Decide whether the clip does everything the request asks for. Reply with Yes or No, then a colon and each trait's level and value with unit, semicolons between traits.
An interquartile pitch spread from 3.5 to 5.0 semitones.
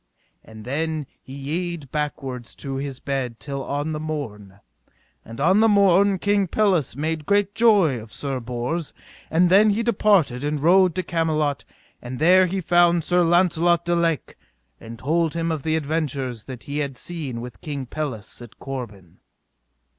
Yes: average, 4.6 semitones